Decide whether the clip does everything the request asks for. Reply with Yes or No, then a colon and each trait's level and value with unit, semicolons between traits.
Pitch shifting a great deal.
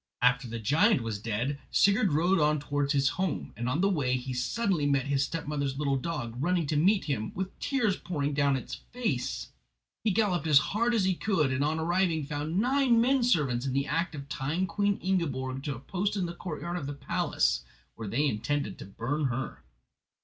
Yes: wide, 5.7 semitones